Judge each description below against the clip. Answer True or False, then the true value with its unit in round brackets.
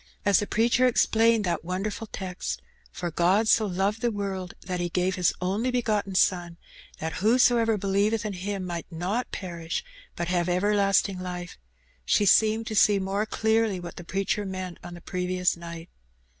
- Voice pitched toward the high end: True (195 Hz)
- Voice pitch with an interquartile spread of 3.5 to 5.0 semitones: False (3.1 semitones)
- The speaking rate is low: False (170 wpm)